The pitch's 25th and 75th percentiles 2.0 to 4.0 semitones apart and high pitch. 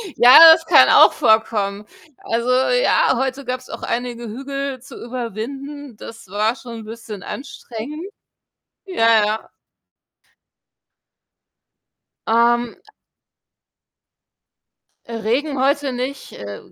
Yes: average, 3.6 semitones; high, 240 Hz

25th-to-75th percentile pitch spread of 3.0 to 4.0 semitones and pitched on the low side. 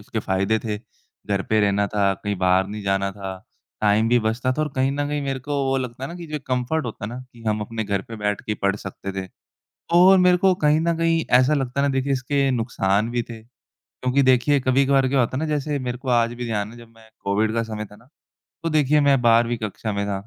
No: average, 4.7 semitones; low, 120 Hz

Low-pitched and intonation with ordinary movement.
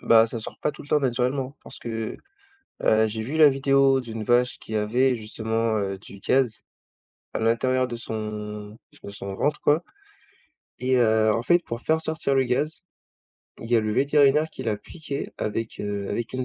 Yes: low, 120 Hz; average, 3.7 semitones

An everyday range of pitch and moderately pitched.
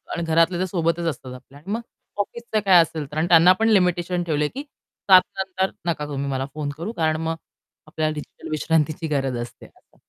Yes: average, 3.2 semitones; medium, 165 Hz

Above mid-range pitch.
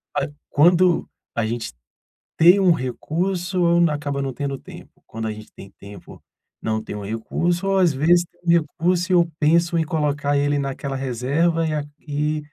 No: medium, 150 Hz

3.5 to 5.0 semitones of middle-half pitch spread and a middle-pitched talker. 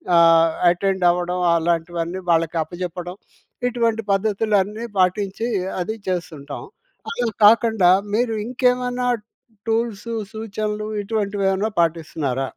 No: average, 4.4 semitones; high, 195 Hz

